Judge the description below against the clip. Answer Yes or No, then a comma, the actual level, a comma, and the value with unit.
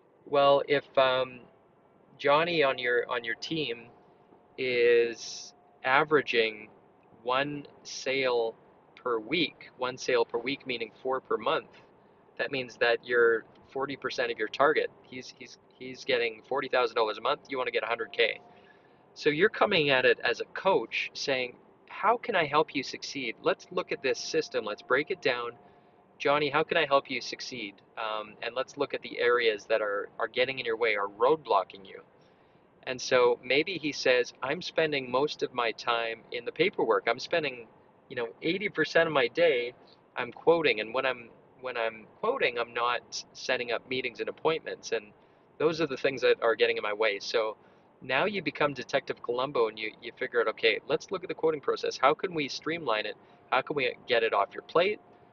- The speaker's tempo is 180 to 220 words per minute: Yes, average, 185 wpm